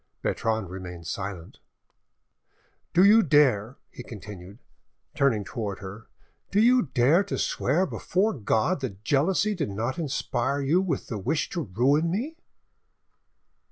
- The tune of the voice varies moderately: No, wide, 8.8 semitones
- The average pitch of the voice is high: No, low, 130 Hz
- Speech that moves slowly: Yes, slow, 125 wpm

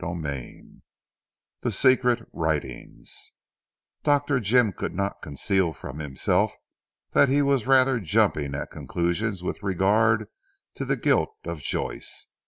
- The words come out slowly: Yes, slow, 125 wpm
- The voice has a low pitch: Yes, low, 100 Hz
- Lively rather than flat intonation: Yes, wide, 8.0 semitones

